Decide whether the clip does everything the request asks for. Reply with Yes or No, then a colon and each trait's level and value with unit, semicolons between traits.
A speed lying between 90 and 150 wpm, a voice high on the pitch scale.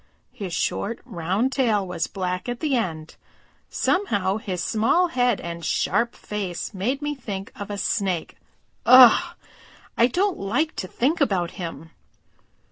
Yes: average, 140 wpm; high, 210 Hz